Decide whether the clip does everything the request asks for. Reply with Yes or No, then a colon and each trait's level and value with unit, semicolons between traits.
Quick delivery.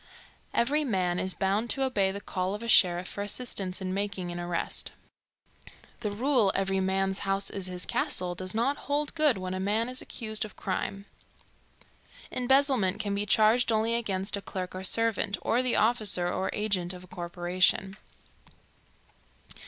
No: average, 165 wpm